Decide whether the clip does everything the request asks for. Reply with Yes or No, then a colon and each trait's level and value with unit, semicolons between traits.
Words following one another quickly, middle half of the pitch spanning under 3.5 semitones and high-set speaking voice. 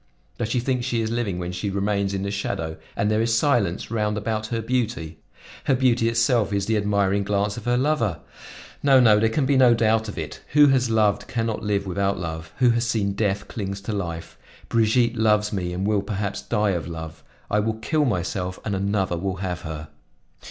No: fast, 210 wpm; average, 3.0 semitones; low, 105 Hz